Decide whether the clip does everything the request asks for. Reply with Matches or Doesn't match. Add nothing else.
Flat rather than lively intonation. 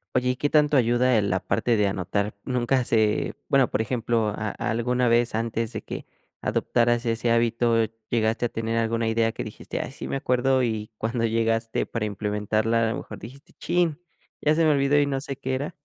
Matches